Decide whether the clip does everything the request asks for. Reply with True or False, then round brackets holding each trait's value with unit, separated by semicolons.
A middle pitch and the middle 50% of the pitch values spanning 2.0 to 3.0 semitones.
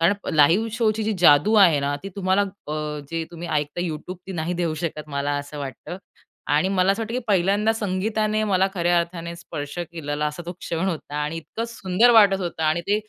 False (175 Hz; 4.6 semitones)